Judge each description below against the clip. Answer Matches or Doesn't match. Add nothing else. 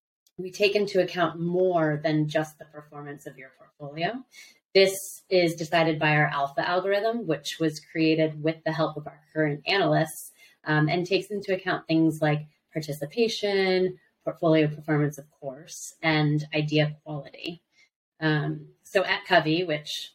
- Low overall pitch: Doesn't match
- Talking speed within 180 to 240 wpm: Doesn't match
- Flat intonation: Doesn't match